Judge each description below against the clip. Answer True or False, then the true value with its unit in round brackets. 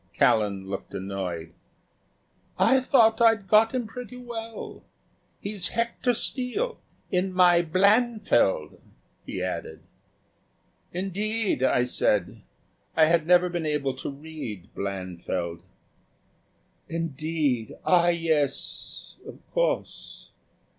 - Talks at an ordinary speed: False (100 wpm)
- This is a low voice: False (170 Hz)